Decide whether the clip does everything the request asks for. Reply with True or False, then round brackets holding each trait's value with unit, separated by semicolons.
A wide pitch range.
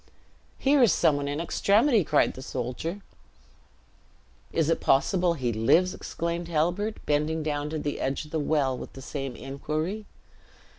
False (3.7 semitones)